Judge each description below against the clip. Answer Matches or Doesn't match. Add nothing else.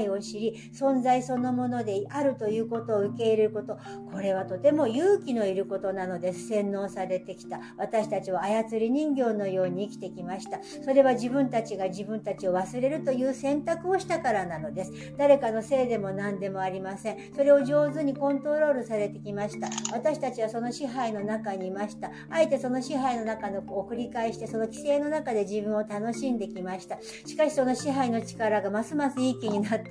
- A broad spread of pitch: Doesn't match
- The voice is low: Doesn't match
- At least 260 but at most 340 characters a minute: Doesn't match